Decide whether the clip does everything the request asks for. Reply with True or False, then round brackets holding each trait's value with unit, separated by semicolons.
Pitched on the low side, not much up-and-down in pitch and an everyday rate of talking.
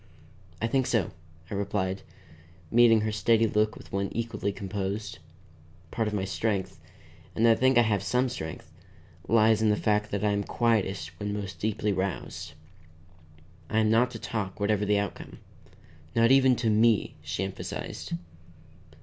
True (105 Hz; 2.3 semitones; 160 wpm)